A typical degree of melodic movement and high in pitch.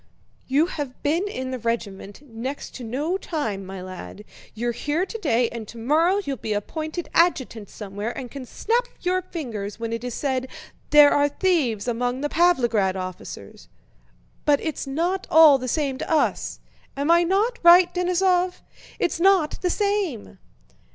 No: wide, 7.0 semitones; very high, 285 Hz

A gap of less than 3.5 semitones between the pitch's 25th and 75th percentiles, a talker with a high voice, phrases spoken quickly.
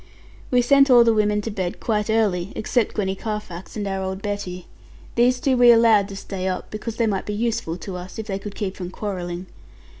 Yes: average, 3.1 semitones; high, 205 Hz; fast, 215 wpm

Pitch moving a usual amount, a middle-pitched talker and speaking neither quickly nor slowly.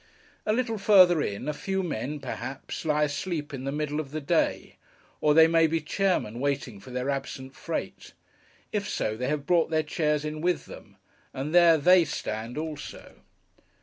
Yes: average, 3.5 semitones; medium, 150 Hz; average, 180 wpm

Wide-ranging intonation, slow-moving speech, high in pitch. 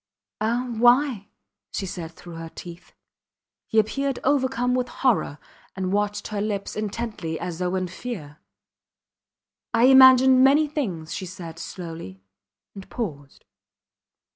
Yes: wide, 6.2 semitones; slow, 125 wpm; high, 205 Hz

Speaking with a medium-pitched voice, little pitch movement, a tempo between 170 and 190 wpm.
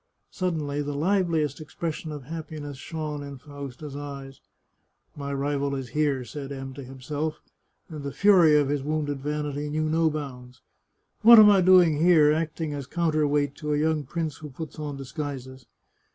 Yes: medium, 150 Hz; narrow, 2.1 semitones; average, 175 wpm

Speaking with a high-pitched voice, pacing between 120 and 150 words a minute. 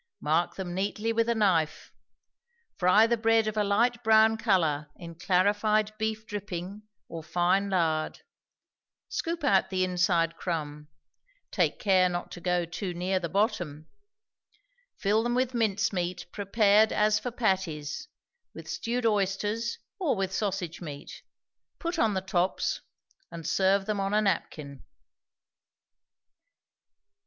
Yes: high, 195 Hz; slow, 135 wpm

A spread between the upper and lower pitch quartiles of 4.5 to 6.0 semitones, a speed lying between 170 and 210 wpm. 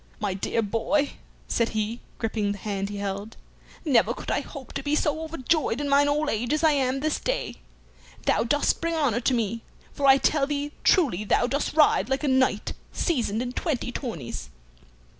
Yes: average, 4.9 semitones; average, 190 wpm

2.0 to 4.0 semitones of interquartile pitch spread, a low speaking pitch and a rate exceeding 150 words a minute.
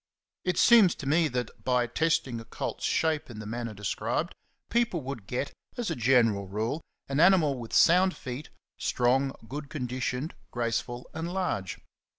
No: average, 5.3 semitones; low, 130 Hz; average, 165 wpm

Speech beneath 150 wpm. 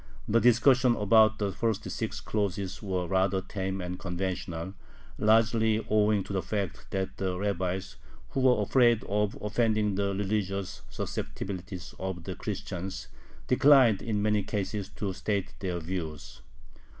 Yes: average, 140 wpm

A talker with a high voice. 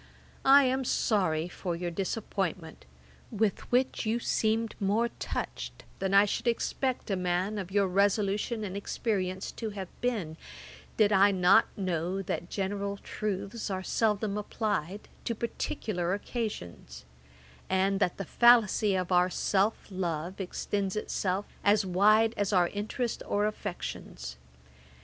Yes: high, 200 Hz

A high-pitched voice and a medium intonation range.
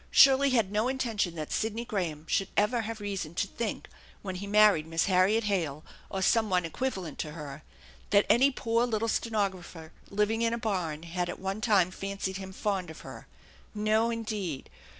Yes: high, 200 Hz; average, 4.0 semitones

